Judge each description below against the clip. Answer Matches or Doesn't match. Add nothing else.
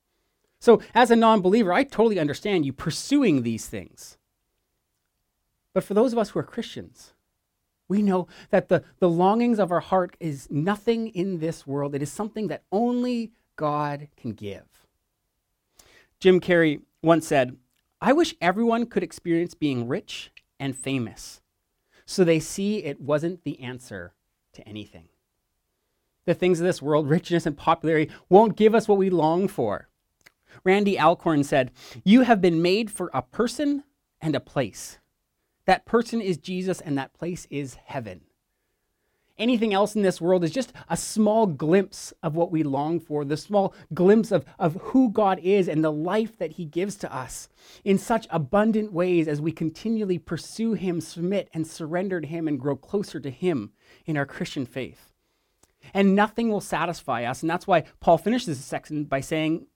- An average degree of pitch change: Matches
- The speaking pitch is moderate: Matches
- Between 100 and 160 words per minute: Doesn't match